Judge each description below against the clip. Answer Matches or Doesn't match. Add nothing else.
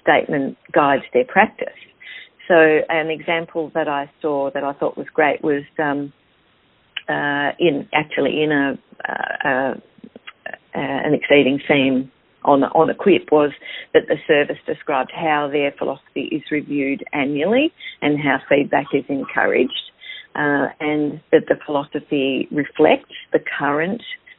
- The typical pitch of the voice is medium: Matches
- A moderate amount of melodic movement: Doesn't match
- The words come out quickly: Doesn't match